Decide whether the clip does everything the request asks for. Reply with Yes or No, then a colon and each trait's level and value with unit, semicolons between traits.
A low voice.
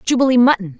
No: high, 240 Hz